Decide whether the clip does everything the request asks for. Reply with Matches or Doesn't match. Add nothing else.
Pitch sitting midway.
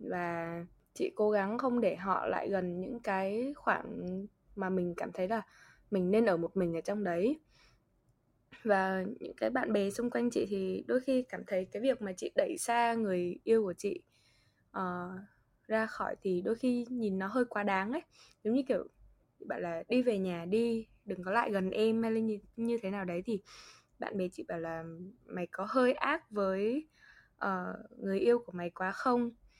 Doesn't match